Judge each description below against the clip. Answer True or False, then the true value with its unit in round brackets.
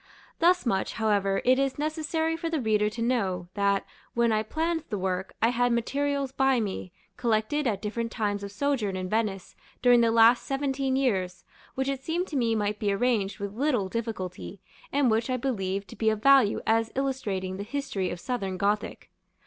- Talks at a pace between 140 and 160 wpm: False (190 wpm)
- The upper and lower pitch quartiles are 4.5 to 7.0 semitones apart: True (4.9 semitones)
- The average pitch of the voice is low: False (230 Hz)